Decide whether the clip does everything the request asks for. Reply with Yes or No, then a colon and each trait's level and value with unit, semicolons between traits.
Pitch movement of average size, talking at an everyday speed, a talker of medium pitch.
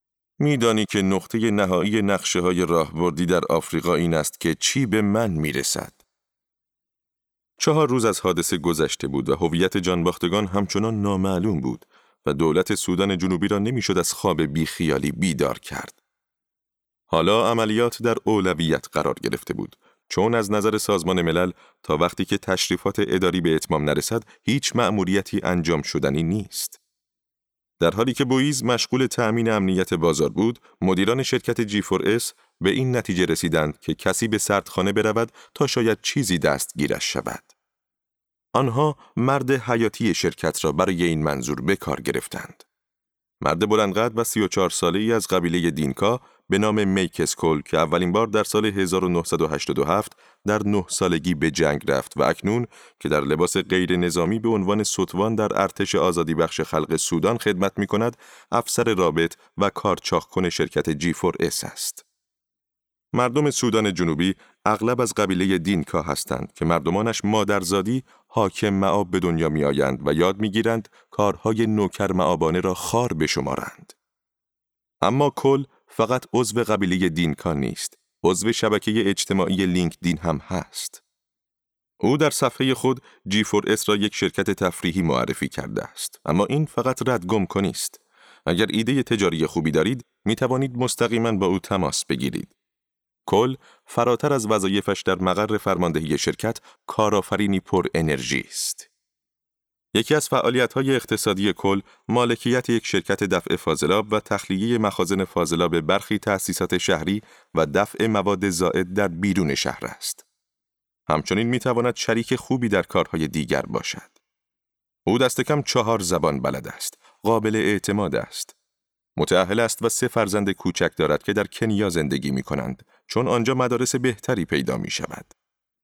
No: average, 4.3 semitones; average, 145 wpm; low, 100 Hz